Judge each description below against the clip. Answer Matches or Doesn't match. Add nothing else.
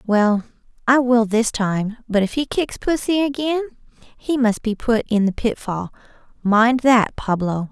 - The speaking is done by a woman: Matches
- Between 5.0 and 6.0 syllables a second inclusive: Doesn't match